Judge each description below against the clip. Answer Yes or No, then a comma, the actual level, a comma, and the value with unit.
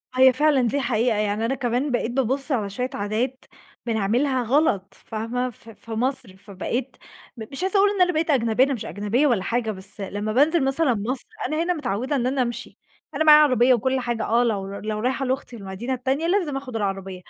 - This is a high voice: Yes, high, 245 Hz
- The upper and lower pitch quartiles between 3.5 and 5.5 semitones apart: Yes, average, 3.9 semitones